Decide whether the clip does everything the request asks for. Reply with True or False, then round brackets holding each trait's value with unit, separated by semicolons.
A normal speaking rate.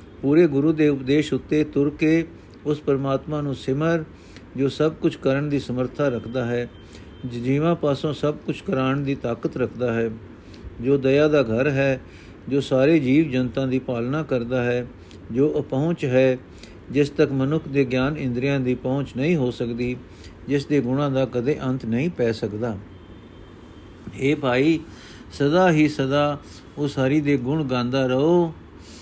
True (155 wpm)